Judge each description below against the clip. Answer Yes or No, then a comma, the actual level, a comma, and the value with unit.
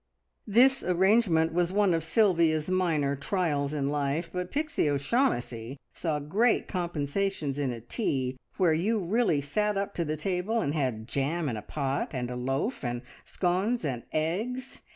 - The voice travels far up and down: Yes, wide, 5.8 semitones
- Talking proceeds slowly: No, average, 160 wpm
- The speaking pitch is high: No, medium, 165 Hz